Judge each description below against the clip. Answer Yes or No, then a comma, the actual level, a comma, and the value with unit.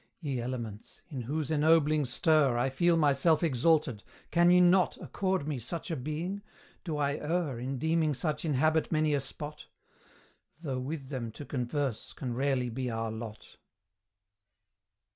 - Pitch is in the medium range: Yes, medium, 145 Hz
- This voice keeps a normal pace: Yes, average, 150 wpm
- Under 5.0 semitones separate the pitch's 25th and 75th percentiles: Yes, average, 3.8 semitones